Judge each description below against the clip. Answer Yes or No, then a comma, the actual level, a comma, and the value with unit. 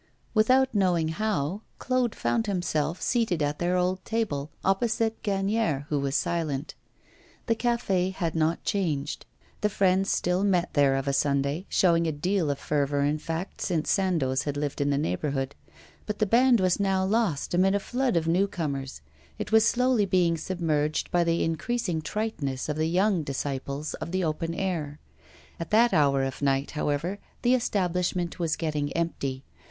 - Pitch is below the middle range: No, medium, 170 Hz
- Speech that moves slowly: No, average, 170 wpm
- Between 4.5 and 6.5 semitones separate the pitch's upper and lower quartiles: Yes, average, 5.3 semitones